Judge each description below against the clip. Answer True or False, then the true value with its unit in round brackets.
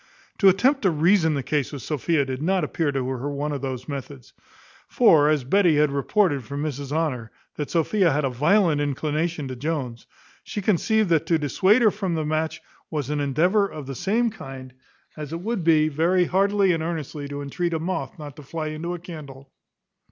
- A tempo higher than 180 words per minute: True (200 wpm)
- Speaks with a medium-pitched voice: True (155 Hz)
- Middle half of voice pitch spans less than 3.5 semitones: False (4.0 semitones)